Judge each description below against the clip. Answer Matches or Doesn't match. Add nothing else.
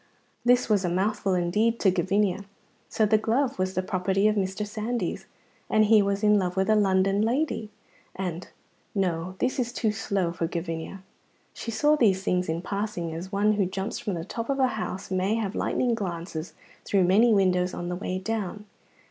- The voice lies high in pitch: Matches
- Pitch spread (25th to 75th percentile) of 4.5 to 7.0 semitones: Doesn't match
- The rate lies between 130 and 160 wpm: Doesn't match